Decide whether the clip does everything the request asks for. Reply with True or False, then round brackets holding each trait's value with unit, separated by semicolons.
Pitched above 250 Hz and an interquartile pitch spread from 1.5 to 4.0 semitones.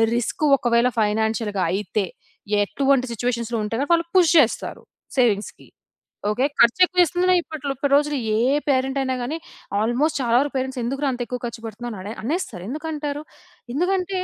False (260 Hz; 4.4 semitones)